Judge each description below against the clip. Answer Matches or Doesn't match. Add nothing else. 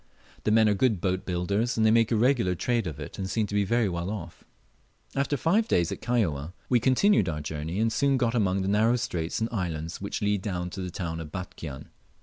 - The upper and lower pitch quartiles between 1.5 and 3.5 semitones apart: Doesn't match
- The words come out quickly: Matches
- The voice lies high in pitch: Doesn't match